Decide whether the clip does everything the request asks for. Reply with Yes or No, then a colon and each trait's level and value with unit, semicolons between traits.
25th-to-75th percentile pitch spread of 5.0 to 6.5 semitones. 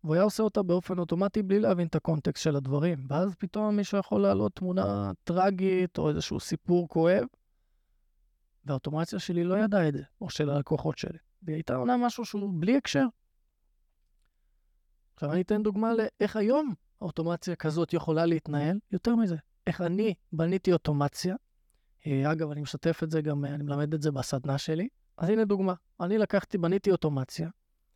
Yes: average, 5.3 semitones